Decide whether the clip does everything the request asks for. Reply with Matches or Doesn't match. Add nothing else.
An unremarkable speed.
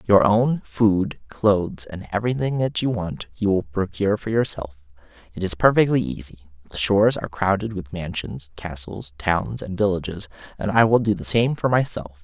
Matches